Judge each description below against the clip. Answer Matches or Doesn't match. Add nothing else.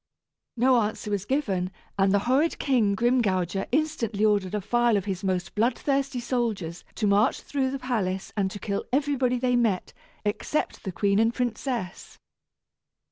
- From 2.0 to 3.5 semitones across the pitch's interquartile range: Doesn't match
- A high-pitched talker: Matches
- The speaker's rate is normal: Matches